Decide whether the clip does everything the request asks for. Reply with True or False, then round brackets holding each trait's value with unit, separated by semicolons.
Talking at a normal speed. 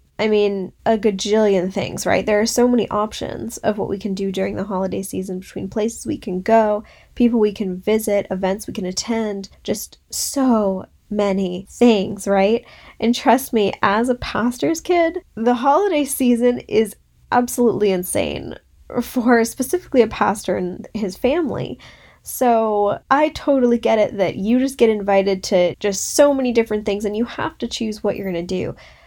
True (175 wpm)